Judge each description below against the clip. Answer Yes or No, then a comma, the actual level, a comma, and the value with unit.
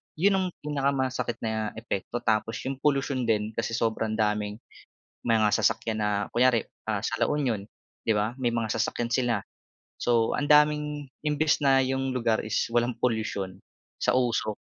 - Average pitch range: Yes, average, 3.3 semitones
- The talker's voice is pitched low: Yes, low, 120 Hz